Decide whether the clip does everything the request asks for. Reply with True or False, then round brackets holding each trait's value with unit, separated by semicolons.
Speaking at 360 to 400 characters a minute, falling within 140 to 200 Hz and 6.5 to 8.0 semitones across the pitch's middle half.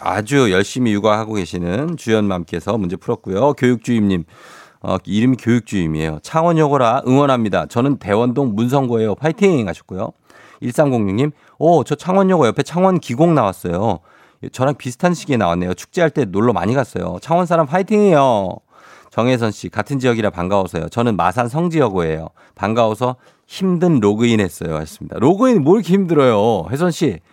False (375 characters per minute; 120 Hz; 7.1 semitones)